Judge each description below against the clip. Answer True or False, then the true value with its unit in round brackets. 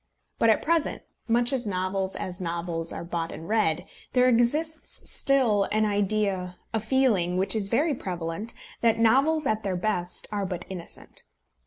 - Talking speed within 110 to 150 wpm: False (160 wpm)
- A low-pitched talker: False (210 Hz)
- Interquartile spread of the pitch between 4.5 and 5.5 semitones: True (4.8 semitones)